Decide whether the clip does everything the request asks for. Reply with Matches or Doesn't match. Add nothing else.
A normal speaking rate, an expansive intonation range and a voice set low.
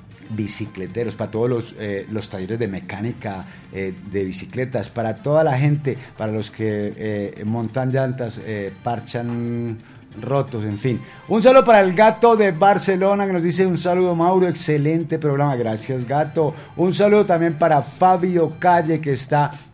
Matches